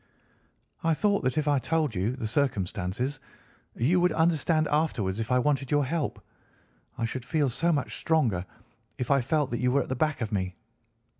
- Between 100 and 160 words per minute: No, average, 190 wpm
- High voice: No, low, 135 Hz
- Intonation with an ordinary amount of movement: Yes, average, 5.0 semitones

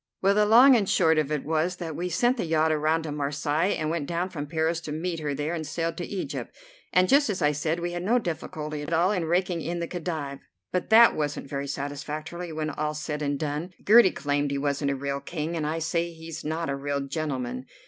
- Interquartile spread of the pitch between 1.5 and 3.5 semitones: Yes, average, 2.9 semitones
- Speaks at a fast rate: Yes, fast, 240 wpm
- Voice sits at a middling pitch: Yes, medium, 160 Hz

